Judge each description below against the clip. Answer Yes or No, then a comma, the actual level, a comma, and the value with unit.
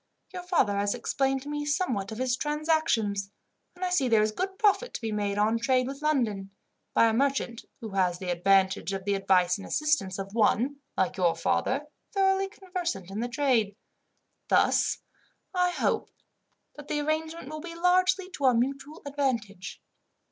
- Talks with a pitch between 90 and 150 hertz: No, very high, 255 Hz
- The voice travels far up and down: Yes, wide, 7.4 semitones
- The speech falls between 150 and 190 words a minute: Yes, average, 175 wpm